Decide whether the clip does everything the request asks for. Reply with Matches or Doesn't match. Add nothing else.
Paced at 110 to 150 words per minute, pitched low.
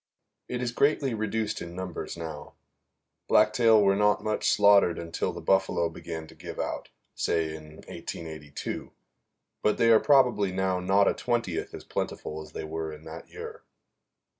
Doesn't match